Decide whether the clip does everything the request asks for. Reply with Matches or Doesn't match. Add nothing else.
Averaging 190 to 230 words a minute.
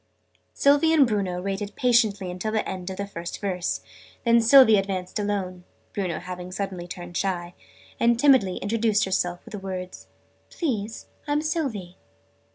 Doesn't match